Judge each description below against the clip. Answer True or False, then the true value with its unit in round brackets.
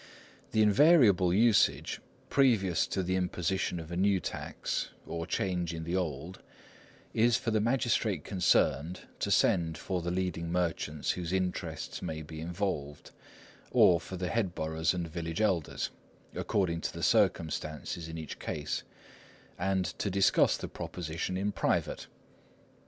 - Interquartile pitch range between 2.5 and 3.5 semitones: True (2.9 semitones)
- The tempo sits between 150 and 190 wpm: False (140 wpm)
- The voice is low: True (90 Hz)